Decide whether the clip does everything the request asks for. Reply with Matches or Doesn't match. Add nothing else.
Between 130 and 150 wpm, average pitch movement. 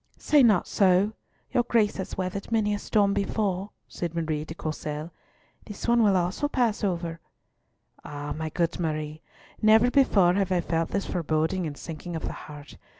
Doesn't match